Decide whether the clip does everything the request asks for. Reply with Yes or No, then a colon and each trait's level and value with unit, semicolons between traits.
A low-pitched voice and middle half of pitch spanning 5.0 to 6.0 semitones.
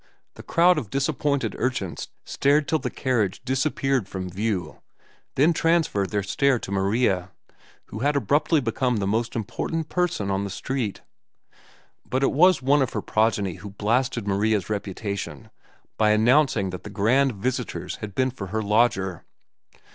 Yes: low, 115 Hz; wide, 5.5 semitones